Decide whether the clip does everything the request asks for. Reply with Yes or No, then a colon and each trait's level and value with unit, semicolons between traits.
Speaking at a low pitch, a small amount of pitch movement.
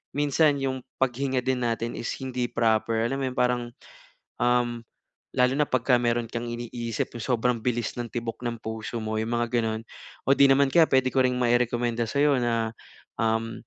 Yes: low, 120 Hz; narrow, 2.0 semitones